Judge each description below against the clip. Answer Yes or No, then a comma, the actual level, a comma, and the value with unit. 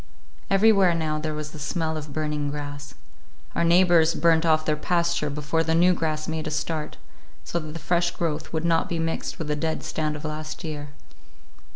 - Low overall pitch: No, medium, 160 Hz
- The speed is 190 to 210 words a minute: Yes, average, 195 wpm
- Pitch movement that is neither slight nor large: No, narrow, 1.7 semitones